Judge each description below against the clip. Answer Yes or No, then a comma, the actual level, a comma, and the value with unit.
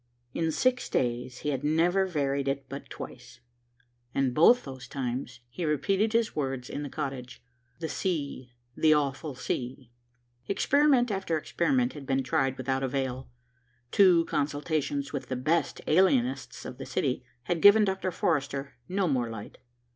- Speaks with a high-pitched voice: No, medium, 145 Hz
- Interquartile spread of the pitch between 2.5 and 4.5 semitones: No, average, 5.1 semitones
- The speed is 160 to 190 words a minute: No, average, 150 wpm